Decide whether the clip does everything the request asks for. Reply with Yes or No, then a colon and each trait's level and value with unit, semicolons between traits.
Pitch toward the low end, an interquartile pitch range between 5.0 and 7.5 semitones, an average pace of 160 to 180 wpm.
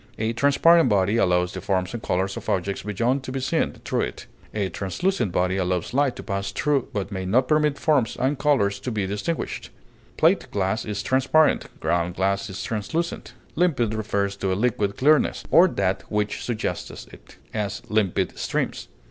Yes: low, 105 Hz; wide, 5.5 semitones; average, 175 wpm